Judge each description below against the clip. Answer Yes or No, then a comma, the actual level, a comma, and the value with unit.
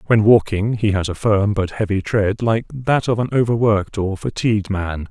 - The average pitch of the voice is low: Yes, low, 105 Hz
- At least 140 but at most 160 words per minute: No, average, 200 wpm